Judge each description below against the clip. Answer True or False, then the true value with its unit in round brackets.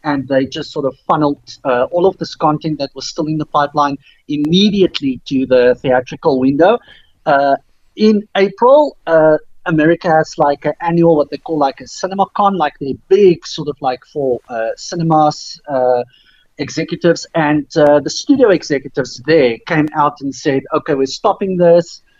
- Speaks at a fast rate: False (170 wpm)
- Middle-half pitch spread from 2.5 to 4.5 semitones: True (3.5 semitones)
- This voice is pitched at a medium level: True (150 Hz)